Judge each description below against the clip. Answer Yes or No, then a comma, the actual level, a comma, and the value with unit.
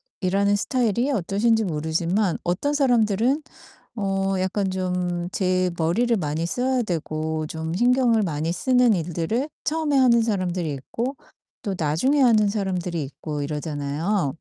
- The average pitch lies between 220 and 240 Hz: No, high, 190 Hz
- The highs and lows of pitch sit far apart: Yes, wide, 6.0 semitones